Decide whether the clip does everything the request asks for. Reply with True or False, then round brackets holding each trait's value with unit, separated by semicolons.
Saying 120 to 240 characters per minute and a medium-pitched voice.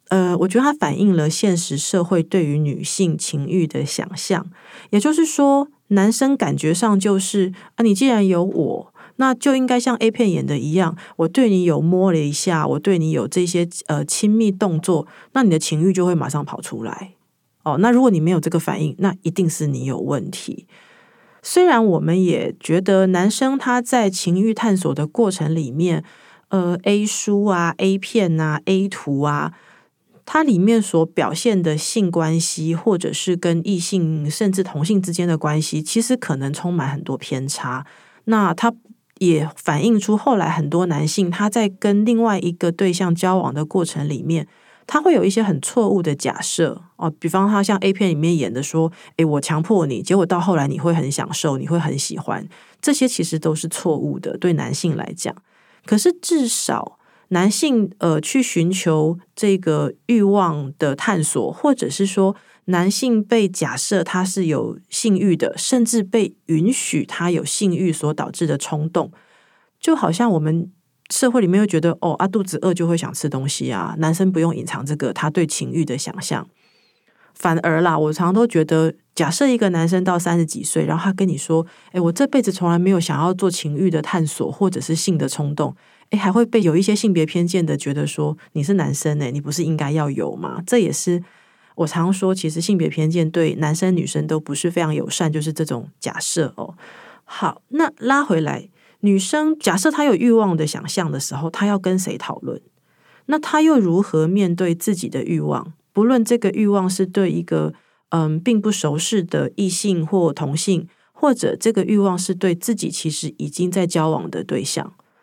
False (270 characters per minute; 180 Hz)